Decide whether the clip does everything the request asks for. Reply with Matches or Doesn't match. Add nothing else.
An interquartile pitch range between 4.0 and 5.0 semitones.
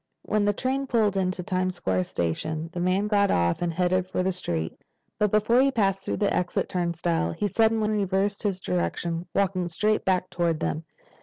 Doesn't match